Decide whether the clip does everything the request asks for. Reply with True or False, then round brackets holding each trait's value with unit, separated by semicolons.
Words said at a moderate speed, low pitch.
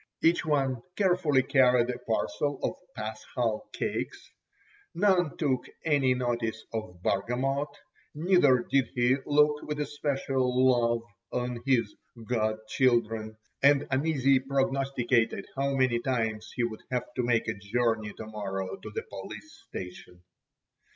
False (130 wpm; 125 Hz)